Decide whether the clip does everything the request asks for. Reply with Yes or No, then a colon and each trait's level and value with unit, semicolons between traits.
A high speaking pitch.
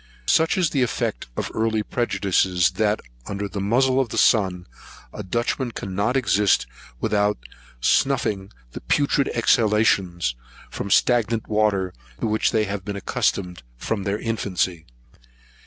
No: low, 105 Hz